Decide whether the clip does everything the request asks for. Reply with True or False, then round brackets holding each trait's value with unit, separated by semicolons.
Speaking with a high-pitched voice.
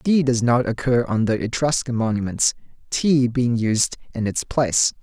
False (120 Hz)